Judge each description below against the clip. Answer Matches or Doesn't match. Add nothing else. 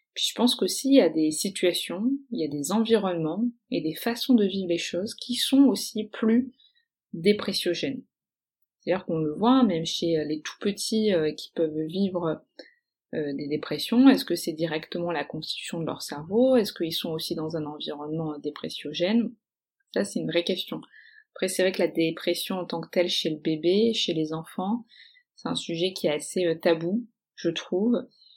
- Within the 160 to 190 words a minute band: Matches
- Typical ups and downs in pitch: Doesn't match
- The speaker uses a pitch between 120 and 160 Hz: Doesn't match